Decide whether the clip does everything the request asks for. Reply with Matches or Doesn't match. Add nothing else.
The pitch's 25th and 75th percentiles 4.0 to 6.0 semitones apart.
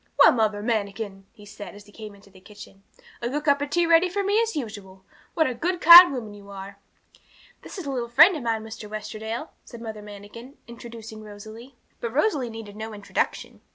Matches